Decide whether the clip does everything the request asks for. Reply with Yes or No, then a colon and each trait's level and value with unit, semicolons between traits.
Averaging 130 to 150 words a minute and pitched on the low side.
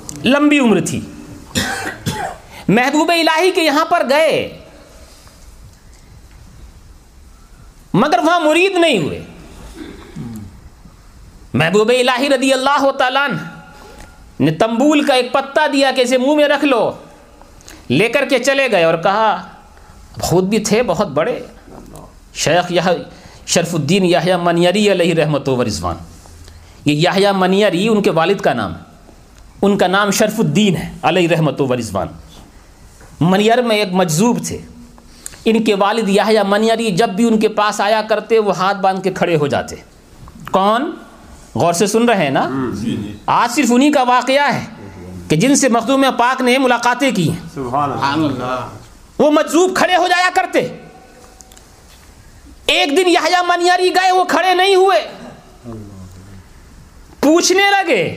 No: average, 140 wpm; high, 210 Hz